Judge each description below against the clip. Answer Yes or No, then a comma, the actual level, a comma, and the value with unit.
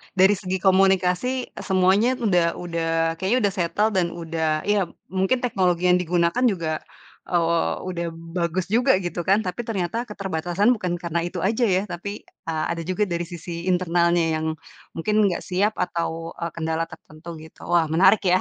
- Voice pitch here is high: No, medium, 180 Hz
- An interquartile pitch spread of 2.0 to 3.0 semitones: Yes, narrow, 2.6 semitones